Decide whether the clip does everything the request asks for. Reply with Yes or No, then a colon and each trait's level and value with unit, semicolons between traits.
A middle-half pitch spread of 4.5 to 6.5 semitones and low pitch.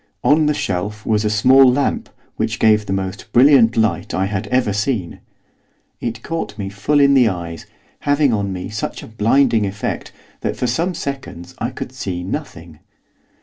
Yes: average, 5.3 semitones; low, 110 Hz